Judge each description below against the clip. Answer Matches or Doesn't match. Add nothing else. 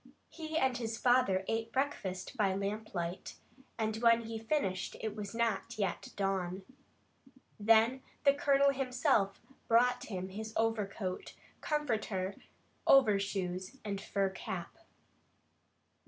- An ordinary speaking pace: Doesn't match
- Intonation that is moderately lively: Matches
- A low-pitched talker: Doesn't match